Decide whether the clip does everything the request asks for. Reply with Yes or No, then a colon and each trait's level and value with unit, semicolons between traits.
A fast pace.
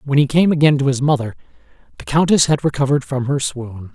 Yes: fast, 215 wpm